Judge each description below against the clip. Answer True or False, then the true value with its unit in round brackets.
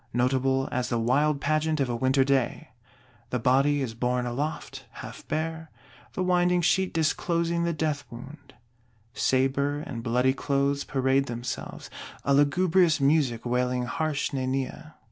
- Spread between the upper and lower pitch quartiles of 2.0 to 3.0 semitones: False (3.5 semitones)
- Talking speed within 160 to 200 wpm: False (140 wpm)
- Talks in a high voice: False (140 Hz)